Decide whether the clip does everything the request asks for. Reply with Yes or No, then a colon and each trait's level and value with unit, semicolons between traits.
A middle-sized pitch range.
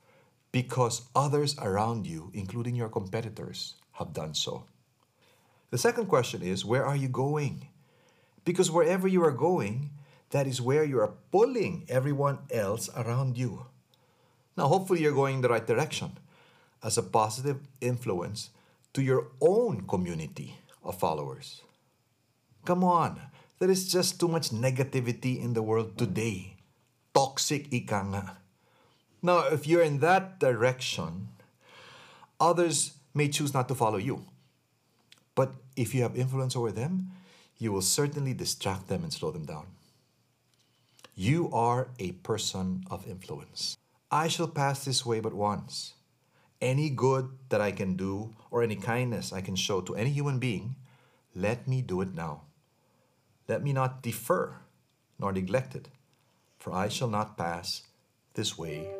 Yes: average, 4.6 semitones